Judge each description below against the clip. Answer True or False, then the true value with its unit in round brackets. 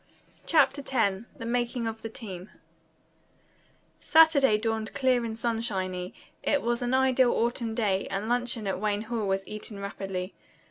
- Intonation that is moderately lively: True (3.4 semitones)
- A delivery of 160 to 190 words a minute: False (145 wpm)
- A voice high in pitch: True (225 Hz)